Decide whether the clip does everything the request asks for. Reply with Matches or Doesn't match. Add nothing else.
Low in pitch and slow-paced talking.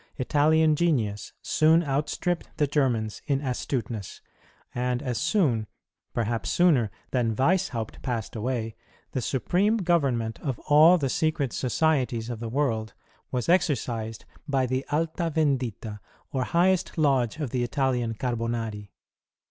Matches